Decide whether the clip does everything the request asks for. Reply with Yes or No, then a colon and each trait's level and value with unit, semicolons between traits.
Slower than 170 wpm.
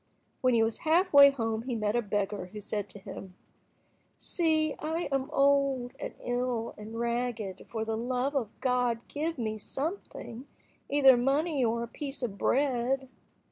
Yes: average, 160 wpm